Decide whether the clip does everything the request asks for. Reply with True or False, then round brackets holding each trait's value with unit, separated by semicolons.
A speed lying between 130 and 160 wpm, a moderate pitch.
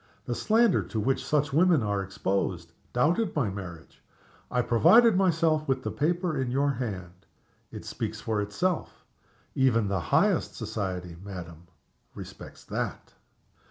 False (135 wpm; 125 Hz)